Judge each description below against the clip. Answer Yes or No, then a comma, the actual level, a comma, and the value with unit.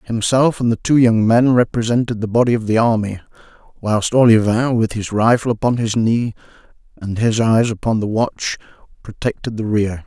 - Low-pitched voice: Yes, low, 115 Hz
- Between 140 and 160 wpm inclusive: No, average, 175 wpm